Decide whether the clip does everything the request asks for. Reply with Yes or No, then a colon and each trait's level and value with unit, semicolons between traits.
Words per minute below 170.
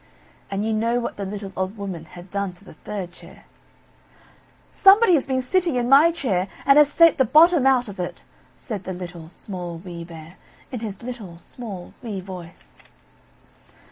No: average, 175 wpm